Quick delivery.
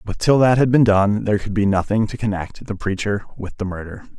Yes: fast, 245 wpm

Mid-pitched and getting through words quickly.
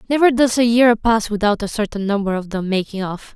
No: high, 215 Hz; fast, 230 wpm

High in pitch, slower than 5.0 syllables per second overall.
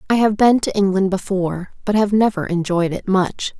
No: high, 195 Hz; 5.2 syllables/s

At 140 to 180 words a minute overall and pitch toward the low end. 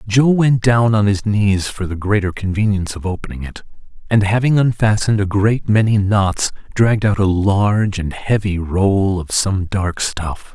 Yes: average, 175 wpm; low, 100 Hz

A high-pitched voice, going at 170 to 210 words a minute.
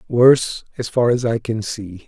No: low, 115 Hz; fast, 205 wpm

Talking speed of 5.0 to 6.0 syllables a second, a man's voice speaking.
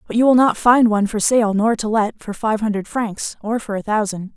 No: 5.3 syllables/s; female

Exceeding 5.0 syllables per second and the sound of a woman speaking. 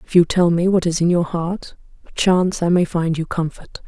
Yes: 5.2 syllables/s; female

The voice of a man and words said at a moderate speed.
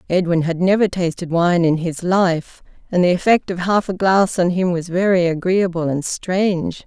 No: female; average, 190 wpm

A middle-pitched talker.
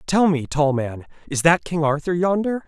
Yes: medium, 160 Hz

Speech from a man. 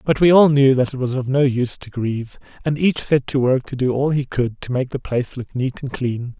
Yes: male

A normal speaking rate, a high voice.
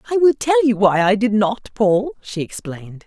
No: fast, 215 wpm; high, 210 Hz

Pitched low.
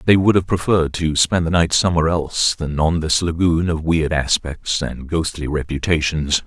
Yes: very low, 80 Hz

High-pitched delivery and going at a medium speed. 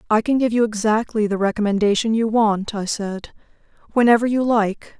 Yes: high, 220 Hz; average, 170 wpm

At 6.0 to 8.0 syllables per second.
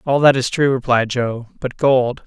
No: 4.4 syllables/s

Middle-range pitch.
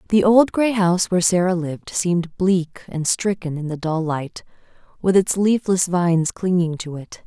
Yes: medium, 180 Hz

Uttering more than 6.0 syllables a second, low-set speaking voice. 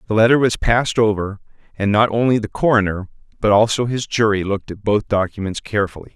Yes: 6.2 syllables/s; low, 105 Hz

